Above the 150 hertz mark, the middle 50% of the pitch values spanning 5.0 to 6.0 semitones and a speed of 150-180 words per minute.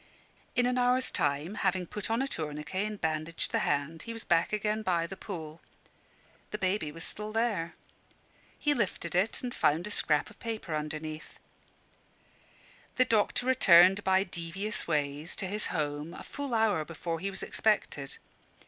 Yes: medium, 185 Hz; average, 5.3 semitones; average, 165 wpm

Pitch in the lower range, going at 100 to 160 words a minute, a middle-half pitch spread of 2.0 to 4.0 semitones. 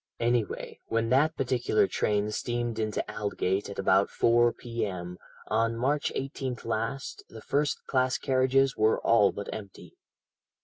Yes: low, 115 Hz; slow, 135 wpm; average, 3.4 semitones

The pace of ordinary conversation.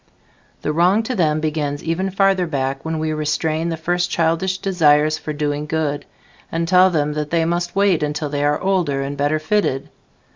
Yes: average, 185 wpm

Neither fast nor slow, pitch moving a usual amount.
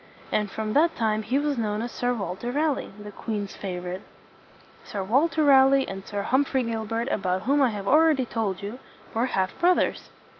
Yes: average, 185 wpm; average, 4.9 semitones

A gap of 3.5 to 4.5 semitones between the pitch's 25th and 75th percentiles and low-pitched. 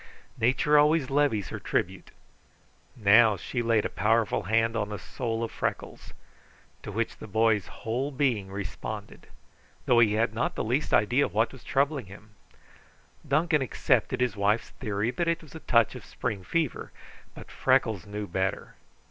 Yes: average, 4.1 semitones; low, 115 Hz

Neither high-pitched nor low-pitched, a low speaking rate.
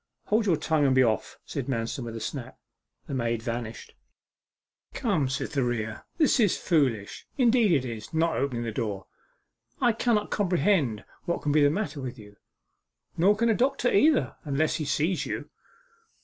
No: medium, 145 Hz; average, 165 wpm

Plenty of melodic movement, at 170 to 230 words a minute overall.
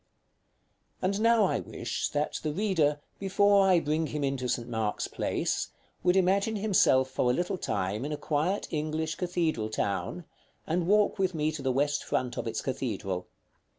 Yes: wide, 6.3 semitones; average, 180 wpm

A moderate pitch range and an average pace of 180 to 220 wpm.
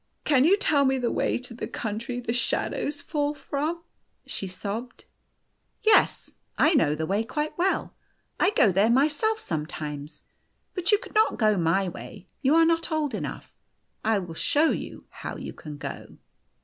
No: wide, 8.0 semitones; average, 185 wpm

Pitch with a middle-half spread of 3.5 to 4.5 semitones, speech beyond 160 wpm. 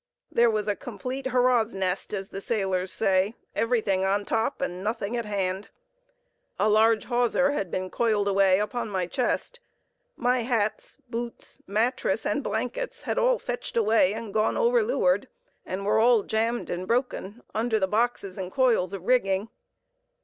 No: average, 3.8 semitones; average, 155 wpm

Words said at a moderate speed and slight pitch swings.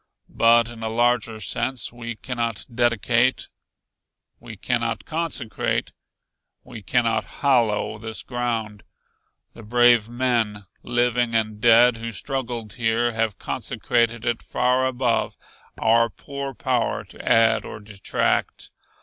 No: slow, 115 wpm; narrow, 1.5 semitones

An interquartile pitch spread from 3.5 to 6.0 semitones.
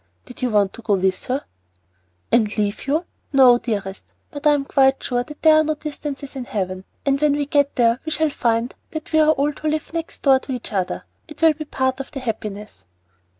Yes: average, 4.7 semitones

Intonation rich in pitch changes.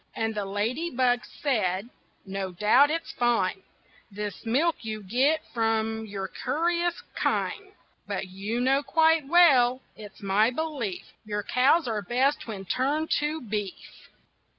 Yes: wide, 6.0 semitones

